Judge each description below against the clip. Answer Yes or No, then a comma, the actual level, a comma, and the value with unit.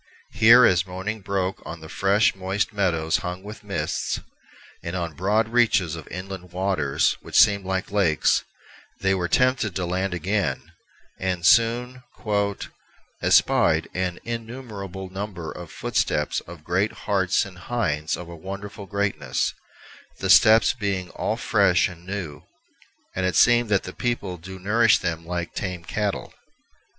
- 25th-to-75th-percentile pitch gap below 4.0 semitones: Yes, average, 2.9 semitones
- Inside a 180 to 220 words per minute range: No, average, 145 wpm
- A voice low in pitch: Yes, very low, 95 Hz